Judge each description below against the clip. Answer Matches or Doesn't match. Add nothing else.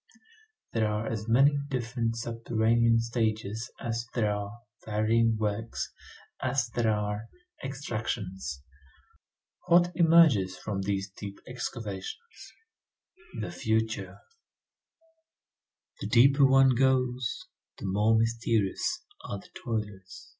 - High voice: Doesn't match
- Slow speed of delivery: Matches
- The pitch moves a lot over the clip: Doesn't match